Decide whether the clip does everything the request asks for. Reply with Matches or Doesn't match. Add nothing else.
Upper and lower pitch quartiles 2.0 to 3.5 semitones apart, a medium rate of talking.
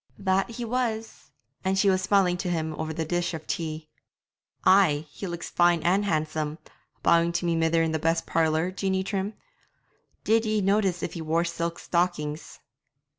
Matches